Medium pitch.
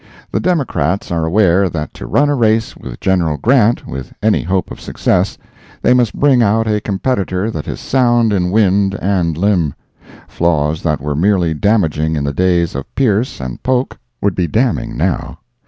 No: very low, 95 Hz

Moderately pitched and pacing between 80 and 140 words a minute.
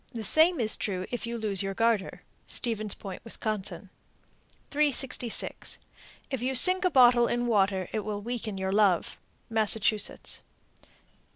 No: high, 220 Hz; slow, 135 wpm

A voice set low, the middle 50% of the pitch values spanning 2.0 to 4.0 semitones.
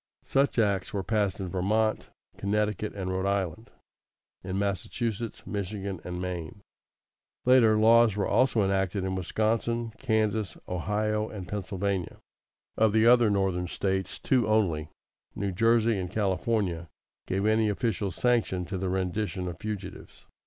Yes: low, 100 Hz; average, 2.8 semitones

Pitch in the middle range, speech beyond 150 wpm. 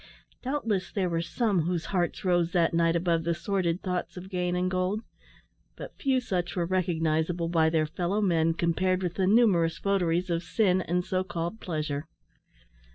Yes: medium, 175 Hz; average, 170 wpm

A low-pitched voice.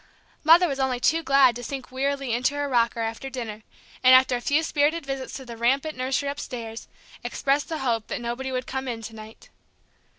No: very high, 260 Hz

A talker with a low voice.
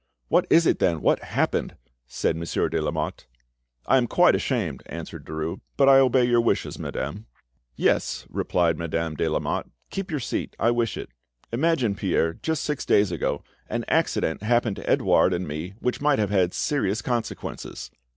Yes: low, 105 Hz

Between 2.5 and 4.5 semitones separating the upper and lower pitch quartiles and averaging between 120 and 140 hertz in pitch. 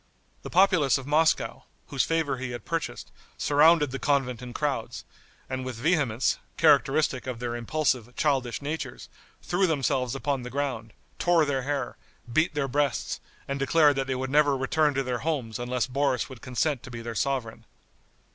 Yes: average, 2.9 semitones; low, 135 Hz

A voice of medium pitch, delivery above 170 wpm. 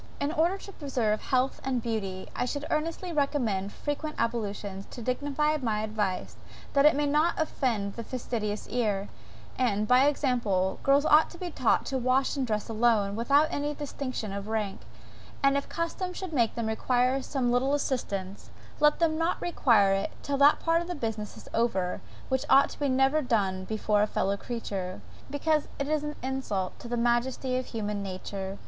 No: very high, 250 Hz; average, 180 wpm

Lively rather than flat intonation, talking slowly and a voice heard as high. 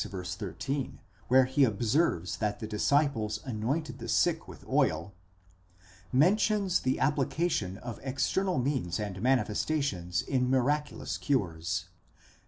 No: wide, 6.3 semitones; slow, 110 wpm; low, 125 Hz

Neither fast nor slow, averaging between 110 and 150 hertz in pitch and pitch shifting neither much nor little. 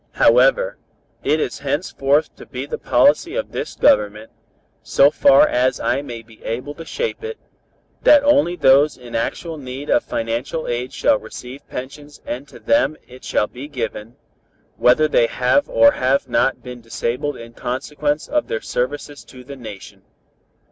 Yes: average, 160 wpm; low, 135 Hz; average, 3.9 semitones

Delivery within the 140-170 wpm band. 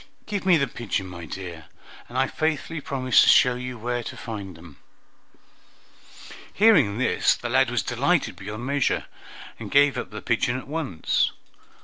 Yes: average, 160 wpm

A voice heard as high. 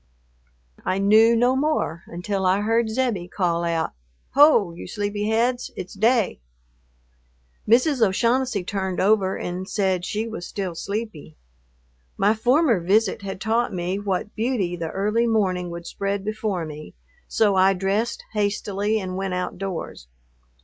Yes: high, 200 Hz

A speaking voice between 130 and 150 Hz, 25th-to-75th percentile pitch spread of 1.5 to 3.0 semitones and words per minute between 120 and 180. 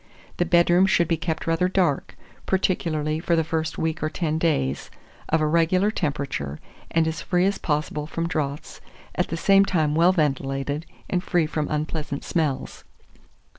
No: medium, 160 Hz; narrow, 2.5 semitones; average, 165 wpm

